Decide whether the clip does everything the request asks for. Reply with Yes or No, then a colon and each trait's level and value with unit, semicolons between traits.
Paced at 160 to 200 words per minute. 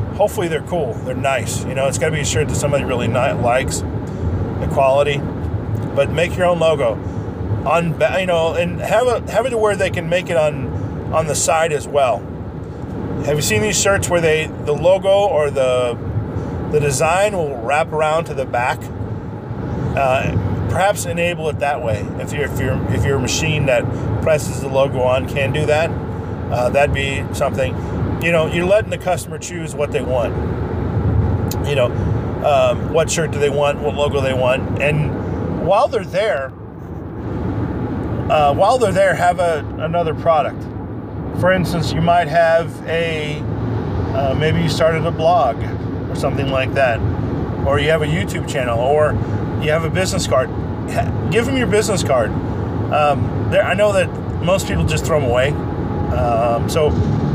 Yes: average, 175 wpm